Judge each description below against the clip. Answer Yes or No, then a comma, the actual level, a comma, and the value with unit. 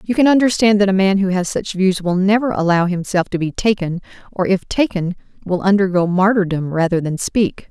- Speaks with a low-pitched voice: No, high, 190 Hz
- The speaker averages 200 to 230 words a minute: Yes, fast, 205 wpm